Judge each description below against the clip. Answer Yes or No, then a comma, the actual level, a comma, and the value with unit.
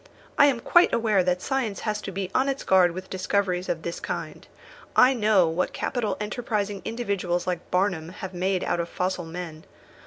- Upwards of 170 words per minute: Yes, average, 185 wpm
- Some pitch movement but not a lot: Yes, average, 3.2 semitones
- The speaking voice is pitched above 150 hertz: Yes, high, 190 Hz